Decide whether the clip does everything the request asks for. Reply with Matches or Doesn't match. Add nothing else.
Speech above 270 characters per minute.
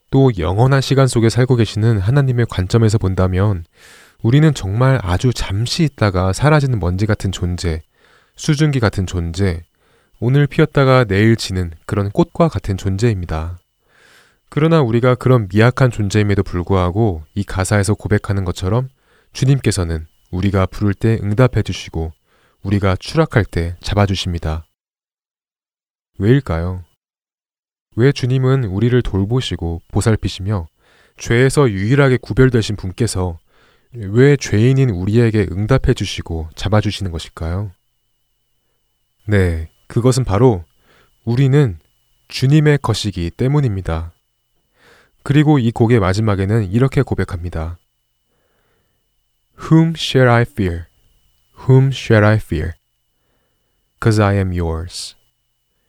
Matches